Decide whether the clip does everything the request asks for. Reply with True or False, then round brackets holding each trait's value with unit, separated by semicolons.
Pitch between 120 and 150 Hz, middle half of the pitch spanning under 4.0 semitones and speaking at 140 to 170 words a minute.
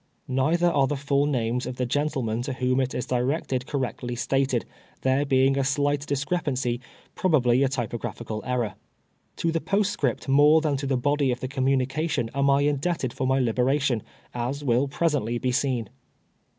False (135 Hz; 2.4 semitones; 180 wpm)